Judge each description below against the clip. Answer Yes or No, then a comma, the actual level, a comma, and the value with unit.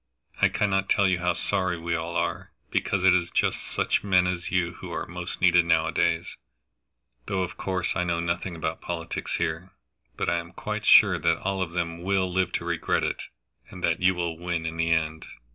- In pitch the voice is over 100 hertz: No, very low, 85 Hz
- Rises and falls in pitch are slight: Yes, narrow, 1.6 semitones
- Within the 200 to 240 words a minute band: Yes, fast, 205 wpm